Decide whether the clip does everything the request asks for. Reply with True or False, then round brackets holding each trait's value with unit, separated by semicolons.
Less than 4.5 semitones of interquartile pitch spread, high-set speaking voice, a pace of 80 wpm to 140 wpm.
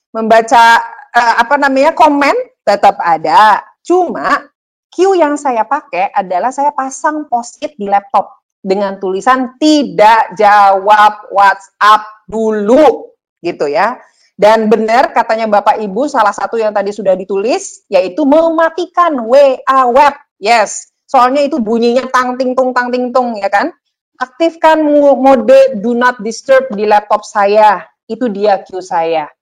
False (5.4 semitones; 250 Hz; 135 wpm)